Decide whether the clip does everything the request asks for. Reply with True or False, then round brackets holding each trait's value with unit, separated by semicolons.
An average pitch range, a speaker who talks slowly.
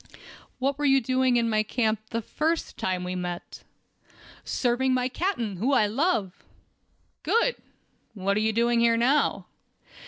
False (3.6 semitones; 150 wpm)